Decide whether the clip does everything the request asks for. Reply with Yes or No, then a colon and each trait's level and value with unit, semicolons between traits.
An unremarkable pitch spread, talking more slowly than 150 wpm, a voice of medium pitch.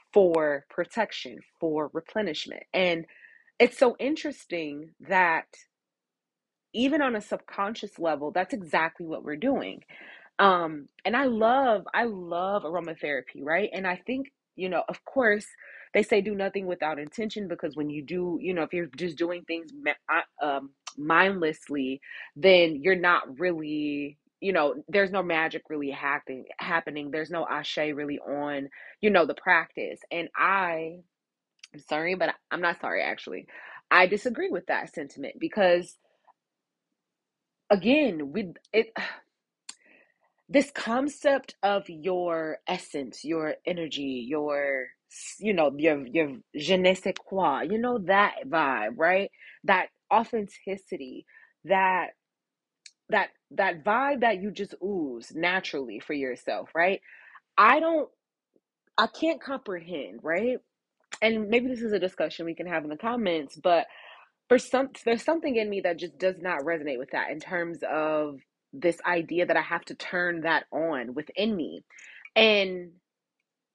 No: wide, 5.7 semitones; average, 140 wpm; medium, 180 Hz